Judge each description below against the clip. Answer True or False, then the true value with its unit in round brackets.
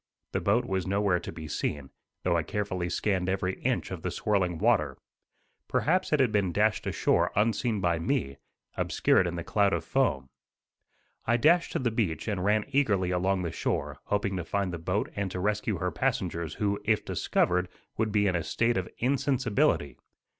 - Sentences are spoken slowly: False (185 wpm)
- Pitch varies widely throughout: False (3.7 semitones)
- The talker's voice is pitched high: False (100 Hz)